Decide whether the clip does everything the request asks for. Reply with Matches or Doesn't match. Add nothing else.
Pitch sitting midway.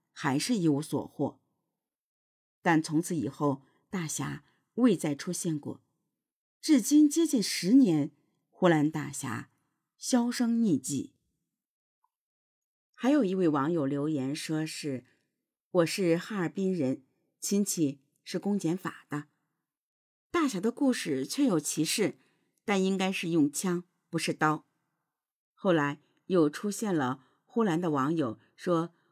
Matches